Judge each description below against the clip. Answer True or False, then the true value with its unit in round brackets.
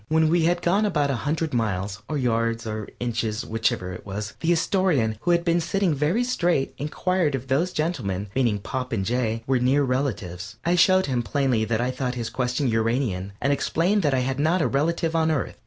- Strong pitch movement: True (6.3 semitones)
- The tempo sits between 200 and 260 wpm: True (205 wpm)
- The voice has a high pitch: False (135 Hz)